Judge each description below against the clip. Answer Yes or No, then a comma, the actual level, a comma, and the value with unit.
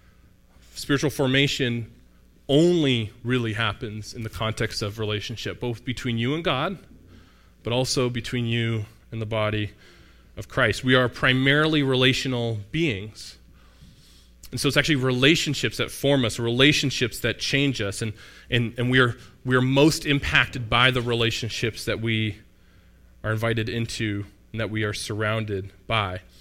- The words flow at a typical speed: Yes, average, 145 wpm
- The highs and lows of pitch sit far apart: No, average, 3.8 semitones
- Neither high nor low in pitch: No, low, 115 Hz